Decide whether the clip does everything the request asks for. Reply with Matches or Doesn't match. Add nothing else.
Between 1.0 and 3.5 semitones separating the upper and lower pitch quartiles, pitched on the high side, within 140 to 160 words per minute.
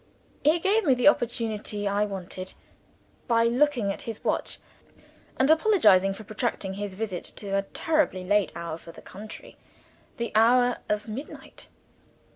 Doesn't match